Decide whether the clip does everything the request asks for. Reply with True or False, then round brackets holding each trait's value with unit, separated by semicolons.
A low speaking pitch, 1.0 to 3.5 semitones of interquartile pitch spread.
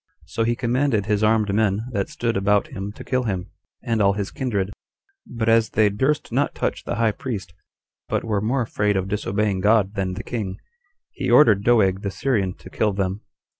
True (105 Hz; 2.7 semitones)